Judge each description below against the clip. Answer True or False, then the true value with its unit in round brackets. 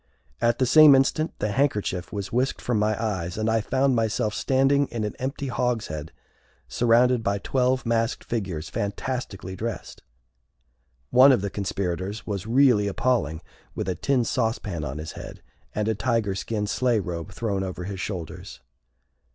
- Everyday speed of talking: True (160 wpm)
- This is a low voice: True (110 Hz)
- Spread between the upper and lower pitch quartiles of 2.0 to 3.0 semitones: False (4.3 semitones)